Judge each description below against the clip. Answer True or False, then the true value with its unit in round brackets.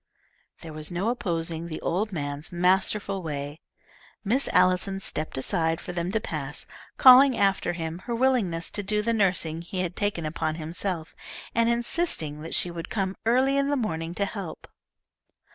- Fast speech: False (165 wpm)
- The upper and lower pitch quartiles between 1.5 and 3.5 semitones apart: False (4.6 semitones)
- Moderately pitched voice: True (180 Hz)